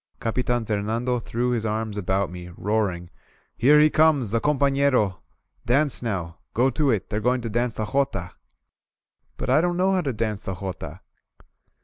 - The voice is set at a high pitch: No, low, 115 Hz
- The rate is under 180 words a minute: Yes, average, 170 wpm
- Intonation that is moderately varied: Yes, average, 4.8 semitones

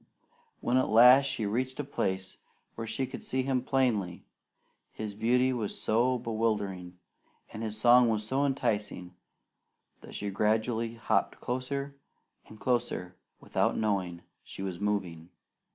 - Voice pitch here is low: Yes, low, 110 Hz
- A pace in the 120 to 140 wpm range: Yes, slow, 135 wpm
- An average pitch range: Yes, average, 3.8 semitones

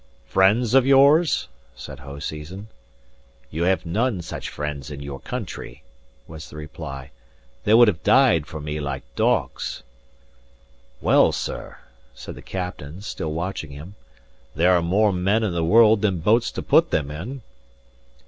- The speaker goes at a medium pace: Yes, average, 150 wpm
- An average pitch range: No, wide, 6.1 semitones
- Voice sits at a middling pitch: No, very low, 85 Hz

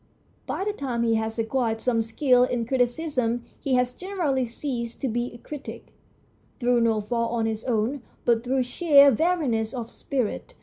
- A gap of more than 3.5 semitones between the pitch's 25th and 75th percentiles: No, average, 3.0 semitones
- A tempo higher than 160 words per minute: Yes, average, 170 wpm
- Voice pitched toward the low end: No, high, 245 Hz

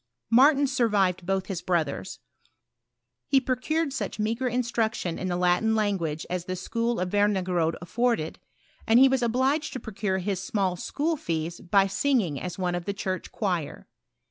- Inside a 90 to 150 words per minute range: No, average, 160 wpm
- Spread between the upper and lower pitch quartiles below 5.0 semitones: No, average, 5.3 semitones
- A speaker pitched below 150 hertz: No, high, 200 Hz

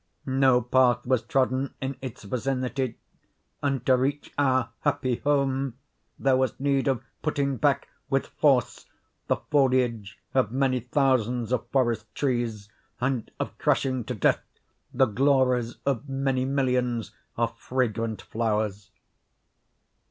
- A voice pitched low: Yes, low, 130 Hz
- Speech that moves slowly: Yes, slow, 125 wpm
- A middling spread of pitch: No, narrow, 2.1 semitones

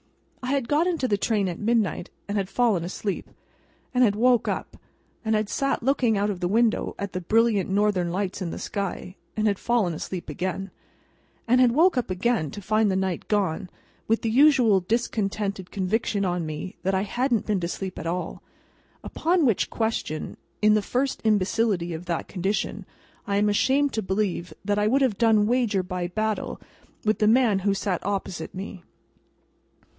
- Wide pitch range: No, average, 3.6 semitones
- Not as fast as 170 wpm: No, average, 180 wpm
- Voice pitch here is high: Yes, high, 205 Hz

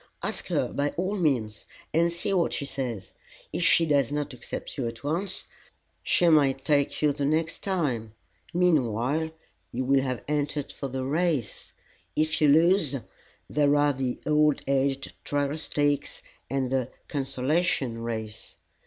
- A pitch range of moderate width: Yes, average, 3.3 semitones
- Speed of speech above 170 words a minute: No, average, 150 wpm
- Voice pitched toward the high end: No, medium, 145 Hz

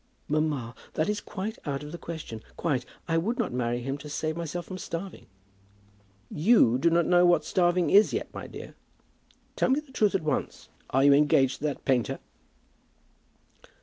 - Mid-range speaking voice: Yes, medium, 160 Hz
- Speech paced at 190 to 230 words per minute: No, average, 180 wpm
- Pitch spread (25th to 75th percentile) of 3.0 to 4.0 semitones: No, average, 4.6 semitones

